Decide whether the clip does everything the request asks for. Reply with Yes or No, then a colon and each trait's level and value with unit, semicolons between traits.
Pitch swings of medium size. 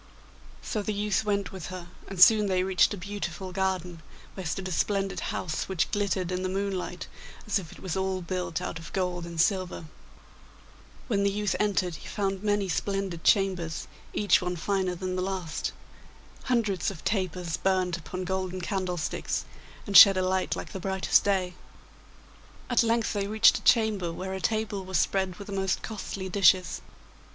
No: narrow, 1.9 semitones